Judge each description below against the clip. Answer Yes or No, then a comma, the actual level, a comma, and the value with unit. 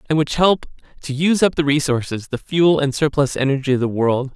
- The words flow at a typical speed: No, fast, 220 wpm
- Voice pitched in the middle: Yes, medium, 145 Hz